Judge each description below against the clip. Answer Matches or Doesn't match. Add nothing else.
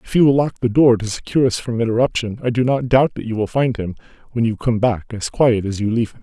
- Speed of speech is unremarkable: Doesn't match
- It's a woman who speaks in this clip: Doesn't match